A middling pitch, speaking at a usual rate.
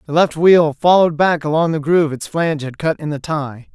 No: medium, 155 Hz; fast, 240 wpm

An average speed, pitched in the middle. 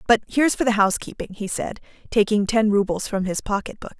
No: average, 195 wpm; high, 210 Hz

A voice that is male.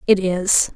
No: female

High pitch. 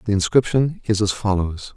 No: low, 105 Hz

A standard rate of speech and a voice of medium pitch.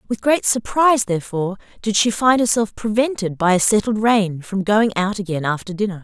No: average, 190 wpm; high, 210 Hz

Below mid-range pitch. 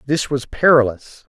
Yes: low, 130 Hz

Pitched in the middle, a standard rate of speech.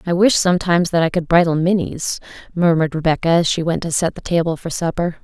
No: medium, 170 Hz; fast, 220 wpm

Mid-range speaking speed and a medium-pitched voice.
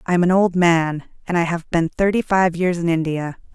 No: fast, 235 wpm; medium, 175 Hz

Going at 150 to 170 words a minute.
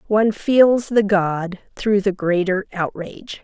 No: average, 140 wpm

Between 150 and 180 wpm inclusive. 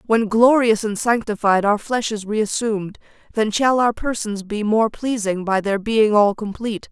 Yes: average, 175 wpm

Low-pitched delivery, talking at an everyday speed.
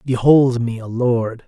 Yes: low, 120 Hz; average, 165 wpm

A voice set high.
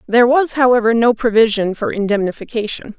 Yes: high, 230 Hz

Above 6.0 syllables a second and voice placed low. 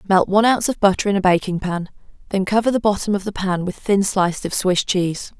No: 6.3 syllables/s; high, 195 Hz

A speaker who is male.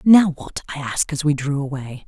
No: female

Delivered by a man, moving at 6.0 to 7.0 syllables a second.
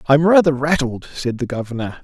Yes: male; 6.1 syllables/s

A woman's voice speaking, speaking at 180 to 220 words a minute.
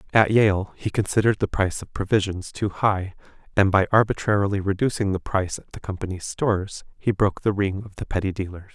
No: male; average, 190 wpm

